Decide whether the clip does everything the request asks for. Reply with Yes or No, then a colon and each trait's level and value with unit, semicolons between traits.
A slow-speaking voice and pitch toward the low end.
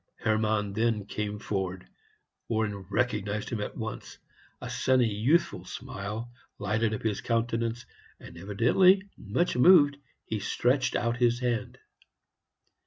Yes: slow, 120 wpm; low, 110 Hz